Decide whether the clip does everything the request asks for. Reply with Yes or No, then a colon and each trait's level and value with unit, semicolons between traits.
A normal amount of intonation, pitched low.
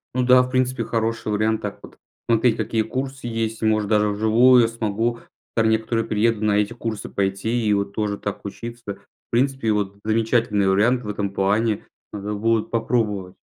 No: narrow, 2.1 semitones; low, 110 Hz